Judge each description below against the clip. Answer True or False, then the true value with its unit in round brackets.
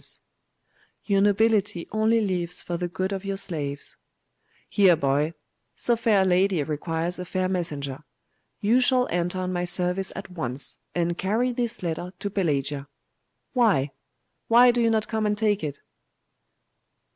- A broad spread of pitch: False (3.9 semitones)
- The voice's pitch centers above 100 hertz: True (185 Hz)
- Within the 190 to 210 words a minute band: False (150 wpm)